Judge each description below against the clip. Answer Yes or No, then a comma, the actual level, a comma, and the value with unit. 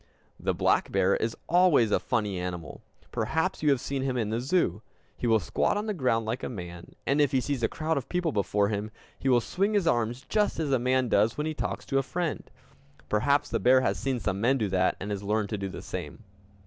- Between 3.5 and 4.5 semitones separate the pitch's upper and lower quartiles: No, wide, 5.4 semitones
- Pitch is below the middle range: Yes, low, 125 Hz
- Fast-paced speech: Yes, fast, 240 wpm